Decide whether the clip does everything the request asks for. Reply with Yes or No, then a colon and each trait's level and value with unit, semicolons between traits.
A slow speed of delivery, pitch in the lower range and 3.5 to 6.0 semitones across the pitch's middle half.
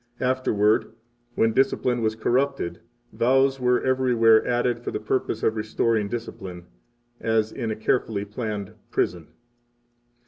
No: slow, 125 wpm; low, 115 Hz; narrow, 2.6 semitones